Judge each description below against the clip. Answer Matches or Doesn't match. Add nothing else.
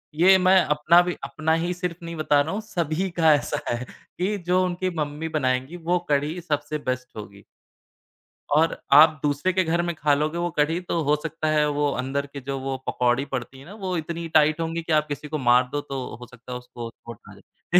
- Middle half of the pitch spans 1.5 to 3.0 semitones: Doesn't match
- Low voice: Doesn't match